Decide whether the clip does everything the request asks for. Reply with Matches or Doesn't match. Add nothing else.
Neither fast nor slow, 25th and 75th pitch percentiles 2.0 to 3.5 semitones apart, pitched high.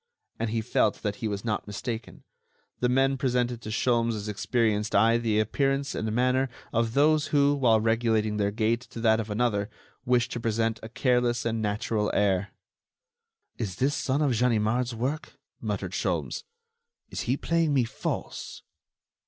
Doesn't match